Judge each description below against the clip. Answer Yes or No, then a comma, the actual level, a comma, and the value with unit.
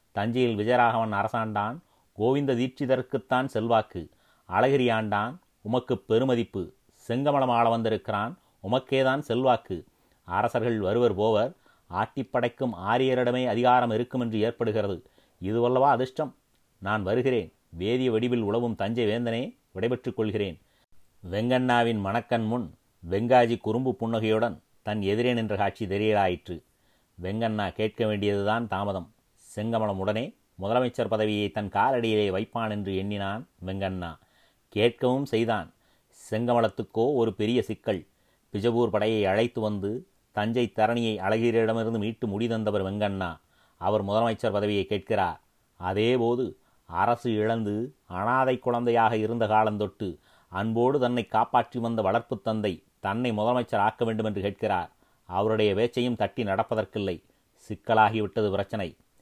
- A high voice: No, low, 110 Hz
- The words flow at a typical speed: Yes, average, 105 wpm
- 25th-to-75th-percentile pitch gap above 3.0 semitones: No, average, 2.7 semitones